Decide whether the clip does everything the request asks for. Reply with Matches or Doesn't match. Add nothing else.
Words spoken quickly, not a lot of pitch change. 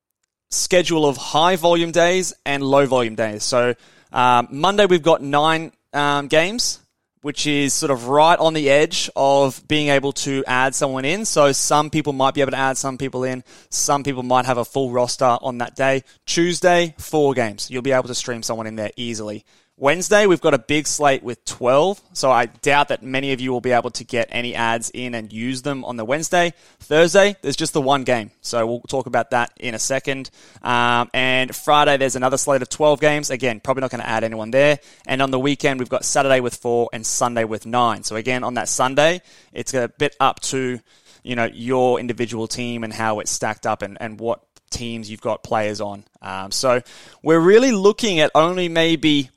Doesn't match